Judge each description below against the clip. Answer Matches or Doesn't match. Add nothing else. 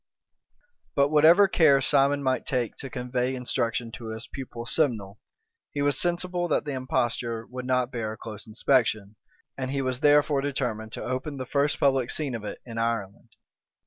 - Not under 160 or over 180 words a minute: Matches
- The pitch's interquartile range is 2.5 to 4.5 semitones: Matches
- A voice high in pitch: Doesn't match